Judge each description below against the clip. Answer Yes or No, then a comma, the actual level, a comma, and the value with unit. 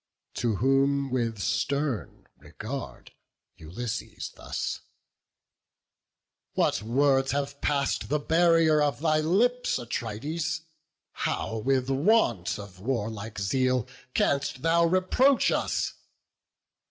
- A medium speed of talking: No, slow, 95 wpm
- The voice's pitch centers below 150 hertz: Yes, low, 135 Hz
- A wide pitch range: No, average, 5.0 semitones